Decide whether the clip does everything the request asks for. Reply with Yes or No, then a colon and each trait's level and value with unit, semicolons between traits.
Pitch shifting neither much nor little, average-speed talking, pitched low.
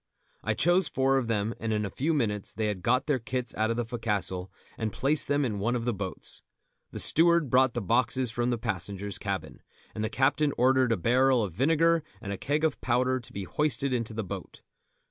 No: average, 3.9 semitones; fast, 220 wpm; low, 120 Hz